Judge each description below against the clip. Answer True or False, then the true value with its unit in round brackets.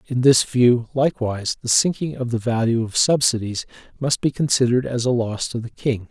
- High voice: False (125 Hz)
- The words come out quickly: False (195 wpm)